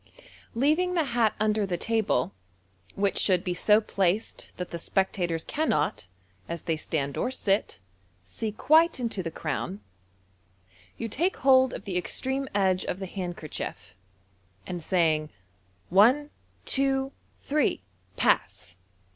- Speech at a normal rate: No, slow, 130 wpm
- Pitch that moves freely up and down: Yes, wide, 7.1 semitones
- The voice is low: No, high, 200 Hz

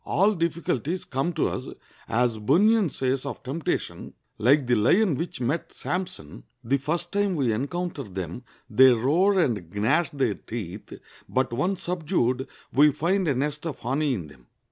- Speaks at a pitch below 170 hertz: Yes, medium, 140 Hz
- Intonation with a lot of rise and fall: Yes, wide, 6.2 semitones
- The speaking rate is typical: Yes, average, 160 wpm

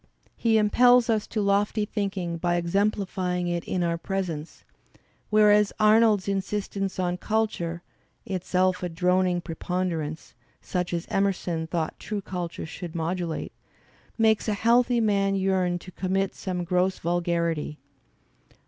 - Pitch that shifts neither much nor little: Yes, average, 3.0 semitones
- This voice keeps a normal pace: No, slow, 130 wpm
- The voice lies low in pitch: No, medium, 185 Hz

